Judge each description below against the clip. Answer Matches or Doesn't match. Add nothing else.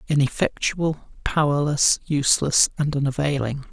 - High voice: Doesn't match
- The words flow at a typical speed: Doesn't match